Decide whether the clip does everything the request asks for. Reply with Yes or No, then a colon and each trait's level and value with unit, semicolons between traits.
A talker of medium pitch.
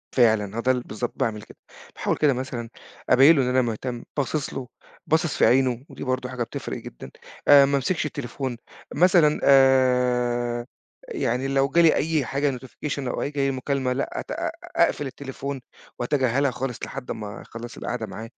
No: low, 130 Hz